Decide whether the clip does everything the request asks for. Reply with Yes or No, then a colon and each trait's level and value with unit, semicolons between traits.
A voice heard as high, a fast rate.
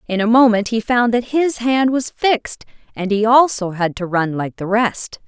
Yes: high, 225 Hz; fast, 215 wpm